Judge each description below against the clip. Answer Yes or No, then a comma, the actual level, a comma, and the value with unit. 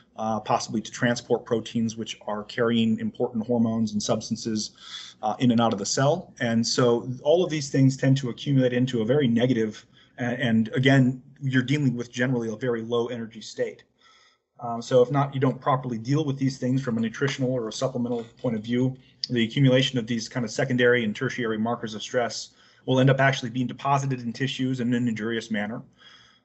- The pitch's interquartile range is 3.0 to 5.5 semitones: No, narrow, 2.4 semitones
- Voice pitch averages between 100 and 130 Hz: Yes, low, 120 Hz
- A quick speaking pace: No, average, 195 wpm